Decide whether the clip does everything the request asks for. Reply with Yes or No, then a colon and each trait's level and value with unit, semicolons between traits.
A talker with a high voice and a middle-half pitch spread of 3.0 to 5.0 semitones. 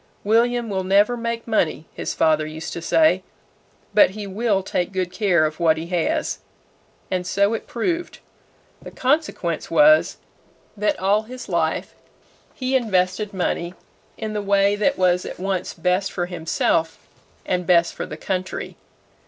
Yes: high, 195 Hz; average, 3.8 semitones